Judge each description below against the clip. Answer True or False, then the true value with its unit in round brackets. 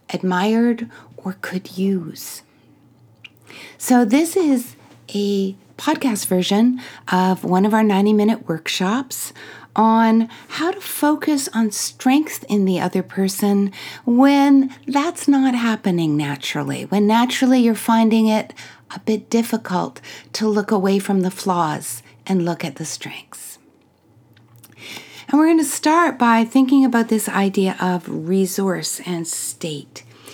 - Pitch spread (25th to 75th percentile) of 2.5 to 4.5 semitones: False (5.1 semitones)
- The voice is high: True (210 Hz)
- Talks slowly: True (130 wpm)